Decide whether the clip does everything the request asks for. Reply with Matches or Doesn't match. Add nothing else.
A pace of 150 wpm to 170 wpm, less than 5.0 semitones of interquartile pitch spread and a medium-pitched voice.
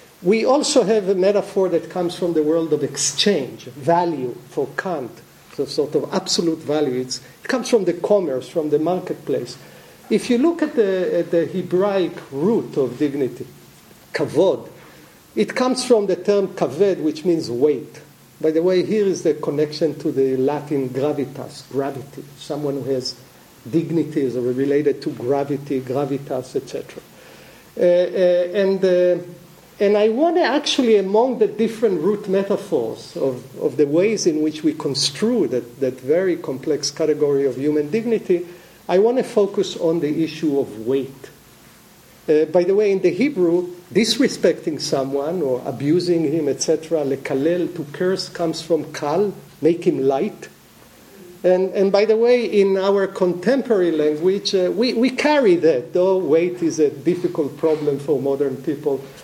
Doesn't match